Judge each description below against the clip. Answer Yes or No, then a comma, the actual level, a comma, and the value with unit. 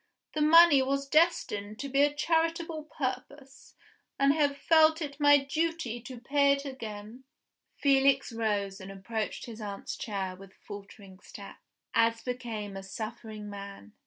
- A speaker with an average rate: Yes, average, 145 wpm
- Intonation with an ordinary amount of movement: No, wide, 5.7 semitones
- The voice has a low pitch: No, very high, 255 Hz